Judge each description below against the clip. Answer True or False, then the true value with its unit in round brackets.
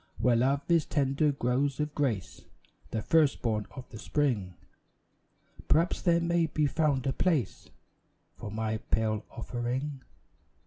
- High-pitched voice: False (135 Hz)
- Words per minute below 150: True (135 wpm)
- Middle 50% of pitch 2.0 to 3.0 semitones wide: False (4.7 semitones)